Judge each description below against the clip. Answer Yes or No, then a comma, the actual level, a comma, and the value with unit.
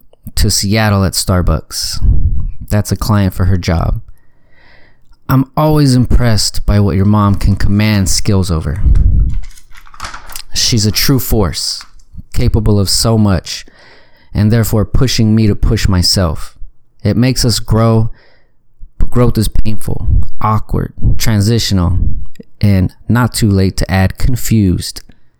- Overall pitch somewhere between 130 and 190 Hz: No, low, 105 Hz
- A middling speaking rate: No, slow, 125 wpm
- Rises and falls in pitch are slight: No, average, 3.4 semitones